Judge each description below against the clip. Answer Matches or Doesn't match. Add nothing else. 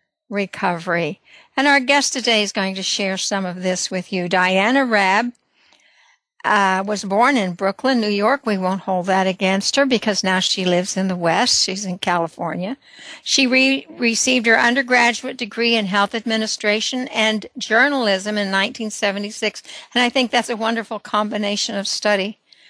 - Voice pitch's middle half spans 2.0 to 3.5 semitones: Doesn't match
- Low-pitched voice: Doesn't match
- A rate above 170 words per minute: Doesn't match